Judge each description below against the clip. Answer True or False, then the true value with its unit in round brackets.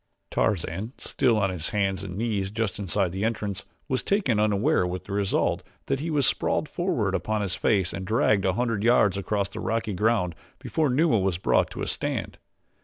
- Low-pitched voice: True (105 Hz)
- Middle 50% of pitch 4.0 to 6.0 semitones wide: False (3.1 semitones)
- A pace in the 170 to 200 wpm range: True (190 wpm)